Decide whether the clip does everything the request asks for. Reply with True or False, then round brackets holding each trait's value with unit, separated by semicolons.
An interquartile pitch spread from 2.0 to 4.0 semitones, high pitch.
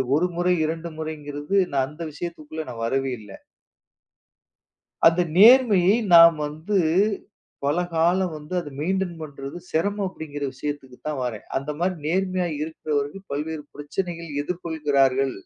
False (3.6 semitones; 160 Hz)